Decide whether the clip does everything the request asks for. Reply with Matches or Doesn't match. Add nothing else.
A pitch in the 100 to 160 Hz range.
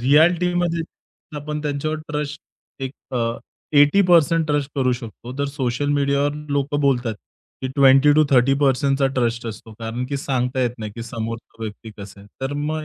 Matches